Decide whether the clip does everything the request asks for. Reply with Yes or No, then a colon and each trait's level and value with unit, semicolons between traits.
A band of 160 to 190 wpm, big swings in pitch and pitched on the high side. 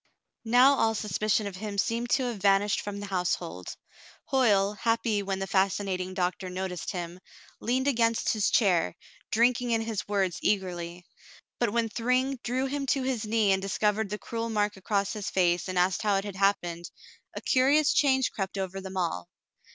No: average, 175 wpm; average, 3.4 semitones; high, 205 Hz